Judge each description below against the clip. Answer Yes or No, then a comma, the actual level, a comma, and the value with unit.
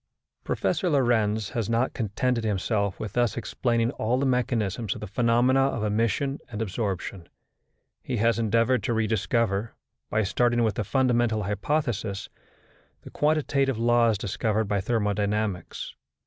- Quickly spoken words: No, slow, 135 wpm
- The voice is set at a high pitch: No, low, 115 Hz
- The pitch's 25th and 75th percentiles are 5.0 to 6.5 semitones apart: No, average, 2.7 semitones